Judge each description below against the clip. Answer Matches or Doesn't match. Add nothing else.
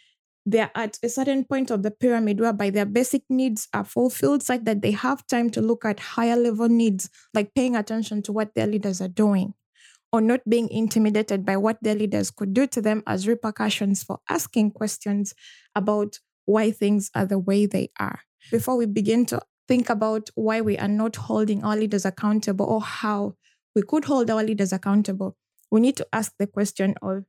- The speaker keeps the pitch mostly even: Matches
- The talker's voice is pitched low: Doesn't match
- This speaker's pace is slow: Doesn't match